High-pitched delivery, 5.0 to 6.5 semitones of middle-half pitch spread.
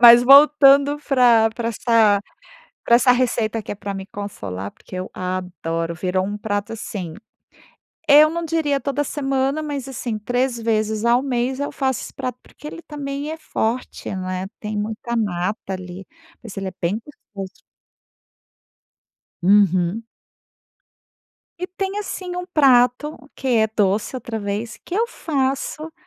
Yes: high, 235 Hz; wide, 5.5 semitones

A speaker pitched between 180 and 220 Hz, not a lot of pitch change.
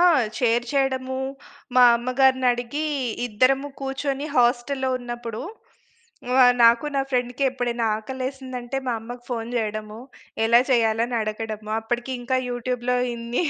No: high, 245 Hz; narrow, 2.0 semitones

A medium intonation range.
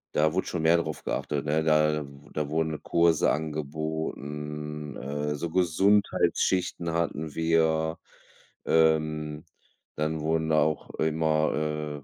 No: narrow, 1.1 semitones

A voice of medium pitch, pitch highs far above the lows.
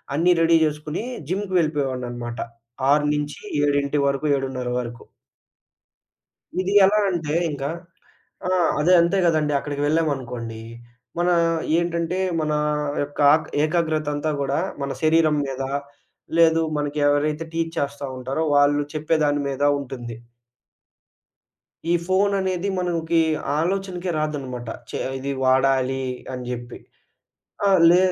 No: medium, 150 Hz; average, 3.4 semitones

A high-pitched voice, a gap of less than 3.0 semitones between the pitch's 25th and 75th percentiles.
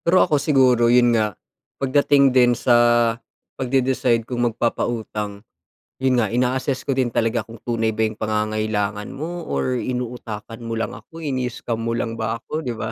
No: low, 120 Hz; narrow, 2.5 semitones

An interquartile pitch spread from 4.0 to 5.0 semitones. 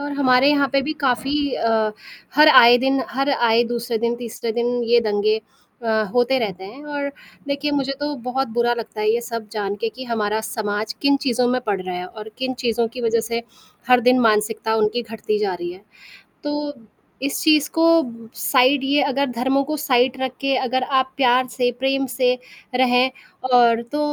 No: average, 3.3 semitones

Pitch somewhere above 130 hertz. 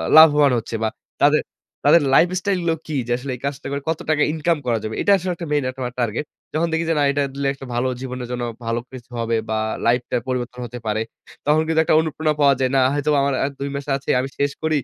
Yes: medium, 140 Hz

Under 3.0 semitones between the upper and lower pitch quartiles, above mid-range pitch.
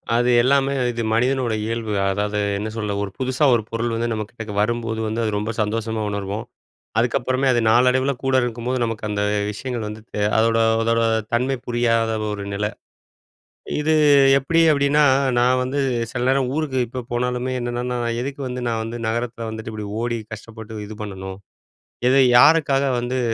No: narrow, 2.5 semitones; low, 120 Hz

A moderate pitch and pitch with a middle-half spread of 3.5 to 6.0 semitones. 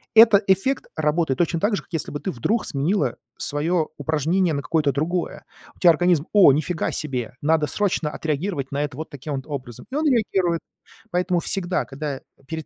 Yes: medium, 160 Hz; average, 4.1 semitones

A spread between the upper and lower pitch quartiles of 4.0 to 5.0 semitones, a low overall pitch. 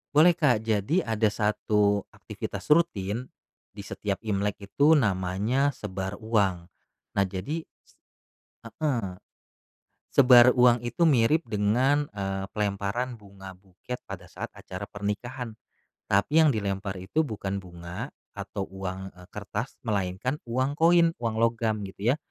Yes: average, 4.5 semitones; low, 105 Hz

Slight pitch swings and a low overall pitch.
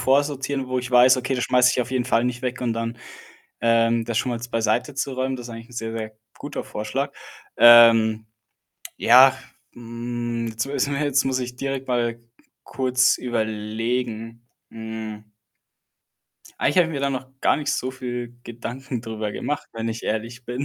Yes: narrow, 2.2 semitones; low, 120 Hz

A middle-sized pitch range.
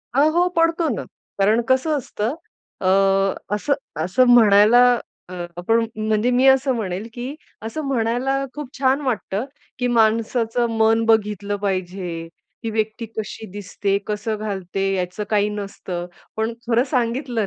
Yes: average, 3.4 semitones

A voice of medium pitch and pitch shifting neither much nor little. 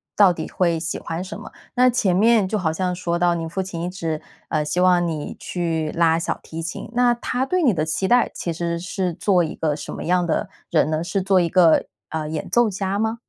Yes: medium, 175 Hz; average, 3.0 semitones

